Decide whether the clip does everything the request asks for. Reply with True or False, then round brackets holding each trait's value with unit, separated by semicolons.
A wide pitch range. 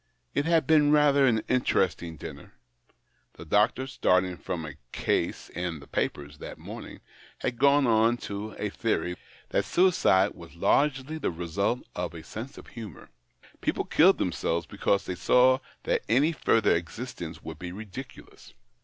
True (7.0 semitones)